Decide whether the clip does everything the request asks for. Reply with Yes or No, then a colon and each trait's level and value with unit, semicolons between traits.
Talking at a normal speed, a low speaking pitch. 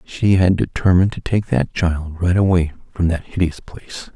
Yes: average, 190 wpm; very low, 90 Hz